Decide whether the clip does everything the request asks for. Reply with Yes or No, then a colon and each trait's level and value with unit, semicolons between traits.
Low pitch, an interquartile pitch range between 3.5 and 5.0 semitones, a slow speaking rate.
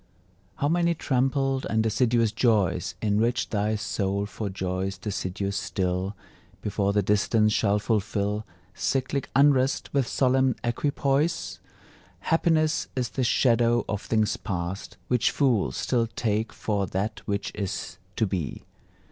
Yes: low, 110 Hz; average, 4.4 semitones; slow, 125 wpm